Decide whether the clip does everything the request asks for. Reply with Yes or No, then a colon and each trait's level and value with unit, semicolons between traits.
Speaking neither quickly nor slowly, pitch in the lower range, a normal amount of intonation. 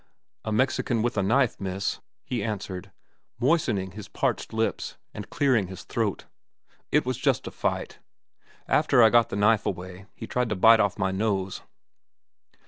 Yes: average, 160 wpm; low, 105 Hz; average, 3.6 semitones